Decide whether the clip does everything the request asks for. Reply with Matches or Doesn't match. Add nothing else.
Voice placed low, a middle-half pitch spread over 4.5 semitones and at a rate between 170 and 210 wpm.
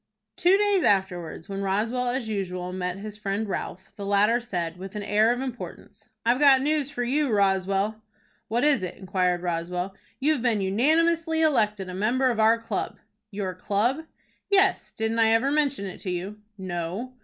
Doesn't match